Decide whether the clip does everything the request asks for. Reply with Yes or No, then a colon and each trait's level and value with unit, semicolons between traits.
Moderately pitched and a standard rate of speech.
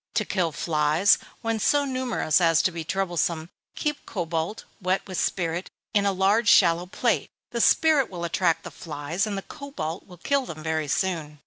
Yes: medium, 180 Hz; average, 180 wpm